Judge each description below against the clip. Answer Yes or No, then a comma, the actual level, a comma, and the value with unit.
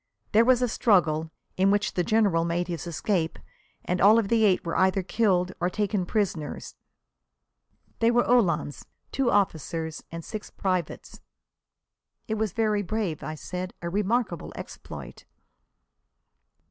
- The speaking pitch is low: No, high, 190 Hz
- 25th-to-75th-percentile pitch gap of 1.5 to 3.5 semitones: No, average, 4.1 semitones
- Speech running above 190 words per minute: No, average, 140 wpm